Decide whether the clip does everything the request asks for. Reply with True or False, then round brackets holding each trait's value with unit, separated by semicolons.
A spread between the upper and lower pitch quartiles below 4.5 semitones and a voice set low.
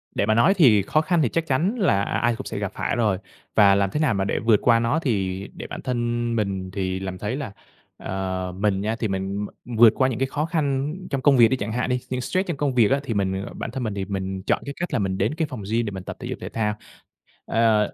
False (5.2 semitones; 115 Hz)